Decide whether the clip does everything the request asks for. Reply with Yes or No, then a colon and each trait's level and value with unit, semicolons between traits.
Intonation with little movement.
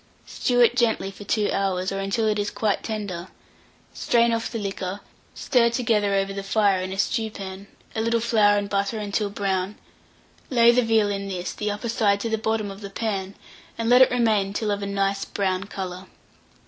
Yes: narrow, 2.3 semitones